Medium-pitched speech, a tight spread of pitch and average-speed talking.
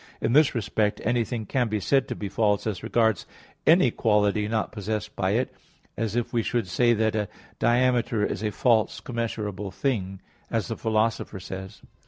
No: low, 110 Hz; narrow, 2.3 semitones; average, 180 wpm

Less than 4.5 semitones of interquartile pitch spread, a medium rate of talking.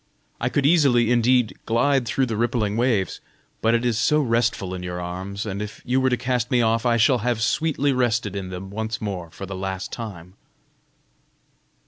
Yes: average, 3.9 semitones; average, 190 wpm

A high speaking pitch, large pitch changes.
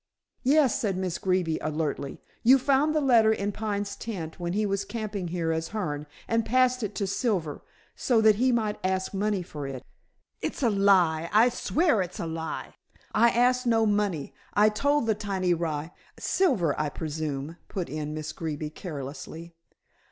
Yes: high, 195 Hz; wide, 5.7 semitones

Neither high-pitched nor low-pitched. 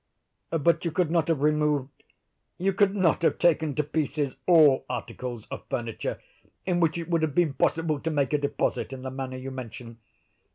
Yes: medium, 150 Hz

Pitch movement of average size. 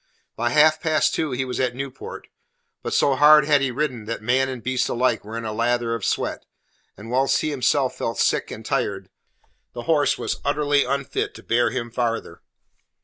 Yes: average, 3.3 semitones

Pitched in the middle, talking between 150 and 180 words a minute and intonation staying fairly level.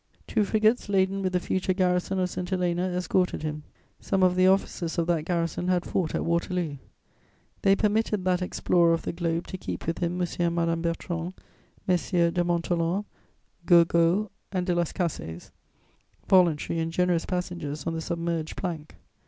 Yes: medium, 175 Hz; average, 170 wpm; narrow, 1.7 semitones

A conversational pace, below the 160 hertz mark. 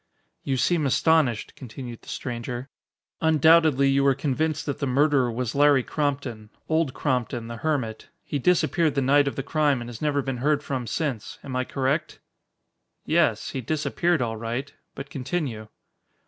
Yes: average, 160 wpm; low, 135 Hz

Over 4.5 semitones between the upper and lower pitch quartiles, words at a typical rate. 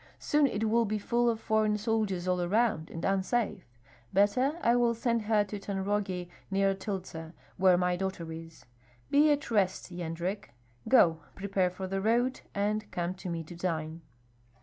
No: average, 3.8 semitones; average, 165 wpm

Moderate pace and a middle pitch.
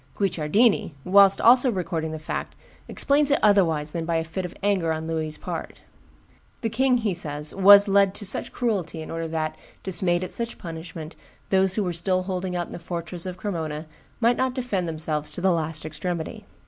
Yes: average, 190 wpm; medium, 180 Hz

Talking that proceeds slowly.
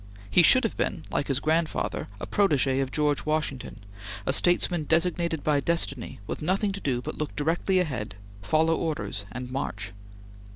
No: average, 165 wpm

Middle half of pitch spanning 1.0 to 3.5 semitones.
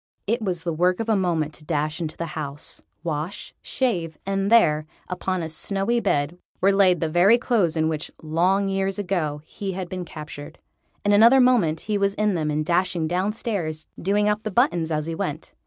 No: average, 4.1 semitones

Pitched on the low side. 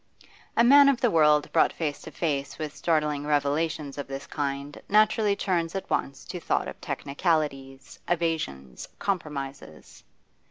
No: medium, 150 Hz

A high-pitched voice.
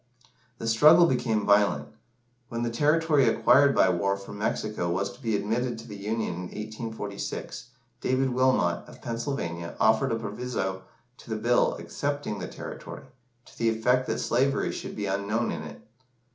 No: low, 110 Hz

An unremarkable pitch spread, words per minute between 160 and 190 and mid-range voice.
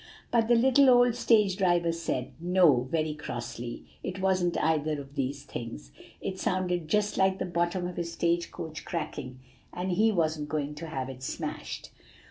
Yes: average, 4.2 semitones; average, 170 wpm; medium, 170 Hz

